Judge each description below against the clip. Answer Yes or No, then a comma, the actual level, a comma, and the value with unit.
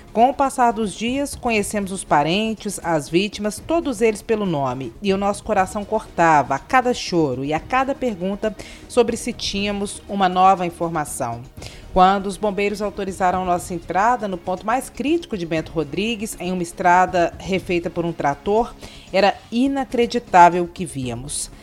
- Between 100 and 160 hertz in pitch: No, high, 195 Hz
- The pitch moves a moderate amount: Yes, average, 4.5 semitones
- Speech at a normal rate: Yes, average, 160 wpm